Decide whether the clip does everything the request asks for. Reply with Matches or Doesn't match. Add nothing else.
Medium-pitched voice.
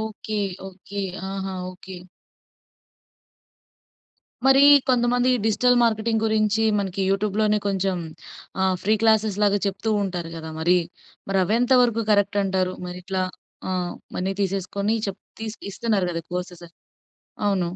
Doesn't match